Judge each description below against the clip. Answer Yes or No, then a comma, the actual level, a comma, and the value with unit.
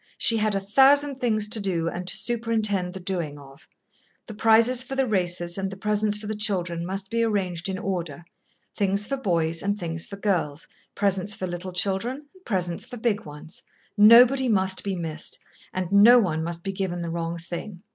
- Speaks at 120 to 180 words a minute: No, average, 195 wpm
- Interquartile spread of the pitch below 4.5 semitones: Yes, average, 3.8 semitones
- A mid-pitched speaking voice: No, high, 195 Hz